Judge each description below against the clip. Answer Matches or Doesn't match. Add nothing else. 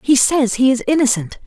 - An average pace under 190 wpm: Doesn't match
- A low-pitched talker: Doesn't match